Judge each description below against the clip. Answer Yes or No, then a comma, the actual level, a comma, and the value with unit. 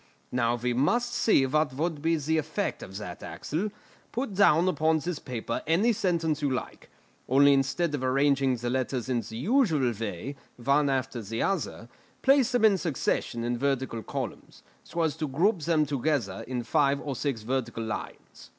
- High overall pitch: No, medium, 140 Hz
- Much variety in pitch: No, average, 4.8 semitones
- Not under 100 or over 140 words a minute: No, average, 175 wpm